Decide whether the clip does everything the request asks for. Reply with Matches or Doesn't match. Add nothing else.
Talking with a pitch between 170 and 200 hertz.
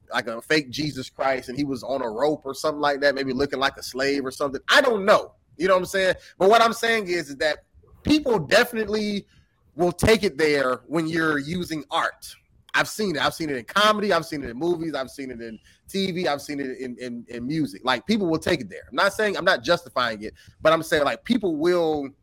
Doesn't match